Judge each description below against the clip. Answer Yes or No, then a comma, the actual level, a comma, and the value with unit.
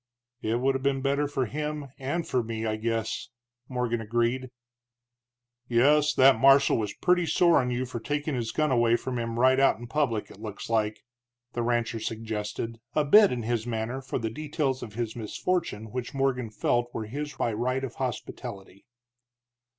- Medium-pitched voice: No, low, 120 Hz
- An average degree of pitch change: Yes, average, 3.3 semitones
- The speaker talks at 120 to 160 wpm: No, average, 180 wpm